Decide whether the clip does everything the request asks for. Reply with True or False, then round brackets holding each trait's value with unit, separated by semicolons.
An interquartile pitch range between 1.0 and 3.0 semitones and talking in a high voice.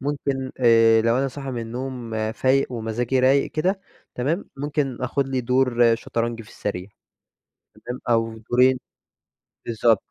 False (2.6 semitones; 125 Hz)